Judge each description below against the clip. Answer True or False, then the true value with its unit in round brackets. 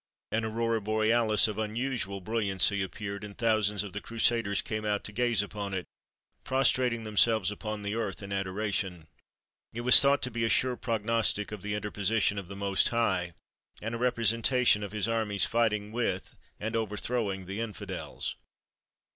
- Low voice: True (110 Hz)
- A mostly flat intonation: True (2.3 semitones)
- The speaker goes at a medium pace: True (165 wpm)